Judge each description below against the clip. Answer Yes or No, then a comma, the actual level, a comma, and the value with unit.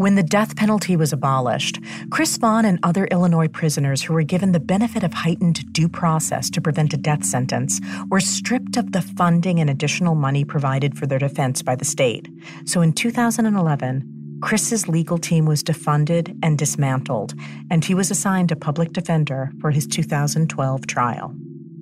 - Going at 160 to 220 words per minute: Yes, average, 170 wpm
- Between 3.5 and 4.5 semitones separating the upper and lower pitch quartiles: Yes, average, 4.2 semitones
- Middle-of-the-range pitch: Yes, medium, 165 Hz